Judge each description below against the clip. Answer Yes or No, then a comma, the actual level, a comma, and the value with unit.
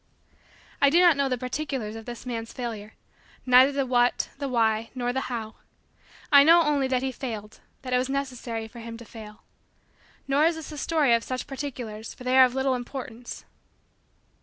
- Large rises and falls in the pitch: No, average, 3.1 semitones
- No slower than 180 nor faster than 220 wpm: Yes, average, 190 wpm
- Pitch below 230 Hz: No, very high, 255 Hz